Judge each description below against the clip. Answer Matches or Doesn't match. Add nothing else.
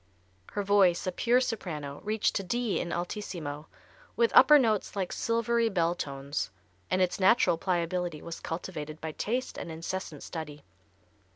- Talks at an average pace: Matches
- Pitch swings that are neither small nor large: Matches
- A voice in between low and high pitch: Matches